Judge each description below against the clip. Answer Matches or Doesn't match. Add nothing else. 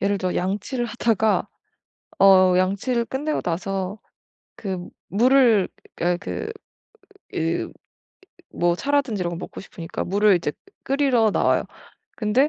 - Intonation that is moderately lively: Matches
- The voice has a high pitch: Matches